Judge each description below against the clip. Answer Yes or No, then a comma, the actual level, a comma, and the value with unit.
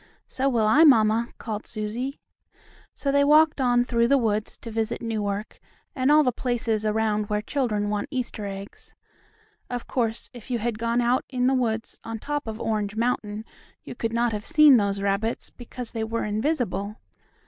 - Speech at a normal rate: Yes, average, 180 wpm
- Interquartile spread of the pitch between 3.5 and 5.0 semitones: No, average, 2.9 semitones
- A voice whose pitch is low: No, high, 230 Hz